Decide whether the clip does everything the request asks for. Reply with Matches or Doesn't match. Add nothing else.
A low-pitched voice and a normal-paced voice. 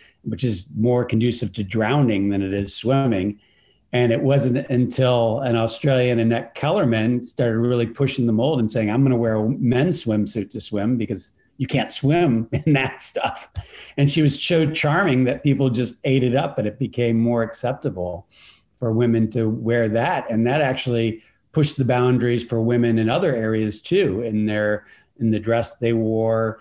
Matches